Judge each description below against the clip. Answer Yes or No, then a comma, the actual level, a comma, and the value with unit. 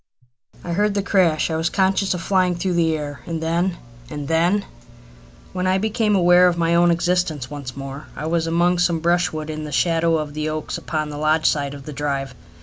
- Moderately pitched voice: Yes, medium, 165 Hz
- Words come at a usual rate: No, fast, 210 wpm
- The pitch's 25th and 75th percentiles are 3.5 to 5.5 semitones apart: No, average, 2.7 semitones